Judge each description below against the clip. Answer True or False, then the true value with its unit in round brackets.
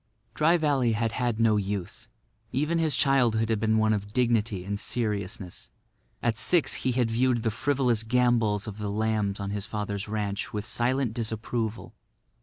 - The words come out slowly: False (165 wpm)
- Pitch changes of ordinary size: True (3.0 semitones)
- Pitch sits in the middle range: False (110 Hz)